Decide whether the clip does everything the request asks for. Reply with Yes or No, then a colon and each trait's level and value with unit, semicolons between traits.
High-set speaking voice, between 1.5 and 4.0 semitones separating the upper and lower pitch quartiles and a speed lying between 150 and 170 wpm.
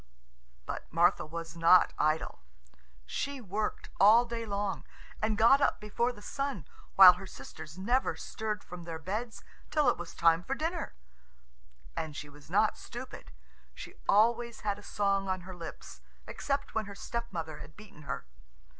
No: high, 200 Hz; wide, 5.6 semitones; average, 160 wpm